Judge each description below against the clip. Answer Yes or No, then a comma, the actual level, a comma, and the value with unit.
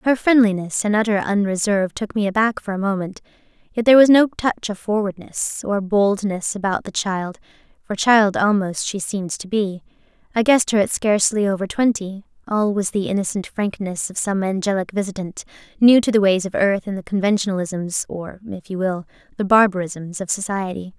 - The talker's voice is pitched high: Yes, high, 200 Hz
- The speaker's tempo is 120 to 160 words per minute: No, average, 175 wpm